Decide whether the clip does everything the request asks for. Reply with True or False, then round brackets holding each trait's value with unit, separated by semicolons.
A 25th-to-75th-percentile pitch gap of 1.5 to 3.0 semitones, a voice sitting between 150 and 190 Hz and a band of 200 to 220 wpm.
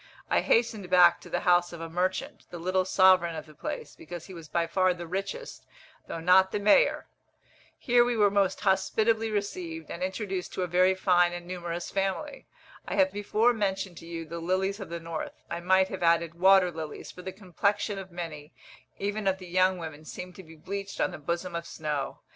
True (2.5 semitones; 185 Hz; 205 wpm)